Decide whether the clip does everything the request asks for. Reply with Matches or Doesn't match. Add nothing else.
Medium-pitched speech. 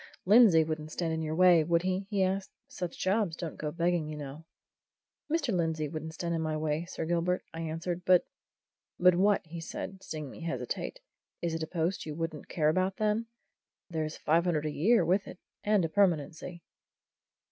Matches